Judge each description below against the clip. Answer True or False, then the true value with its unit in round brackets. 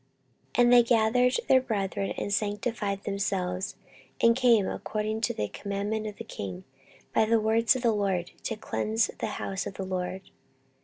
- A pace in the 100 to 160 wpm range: False (170 wpm)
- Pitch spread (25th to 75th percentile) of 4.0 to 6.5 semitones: False (2.6 semitones)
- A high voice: True (210 Hz)